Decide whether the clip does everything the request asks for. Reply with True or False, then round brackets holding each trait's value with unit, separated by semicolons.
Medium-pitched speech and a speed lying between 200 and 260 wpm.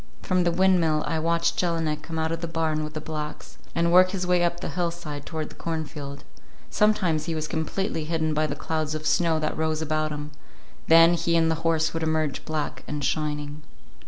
True (160 Hz; 205 wpm)